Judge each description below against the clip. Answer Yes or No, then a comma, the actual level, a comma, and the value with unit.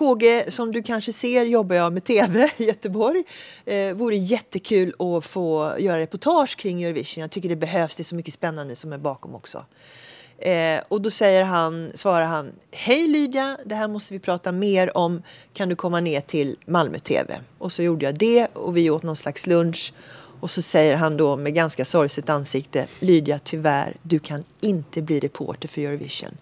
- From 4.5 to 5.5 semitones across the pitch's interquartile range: Yes, average, 4.9 semitones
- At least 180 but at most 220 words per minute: Yes, average, 185 wpm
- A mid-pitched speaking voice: Yes, medium, 175 Hz